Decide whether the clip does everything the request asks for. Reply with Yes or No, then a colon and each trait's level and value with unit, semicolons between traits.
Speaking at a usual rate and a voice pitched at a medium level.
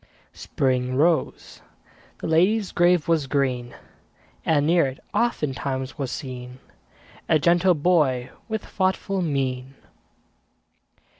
No: slow, 100 wpm; medium, 145 Hz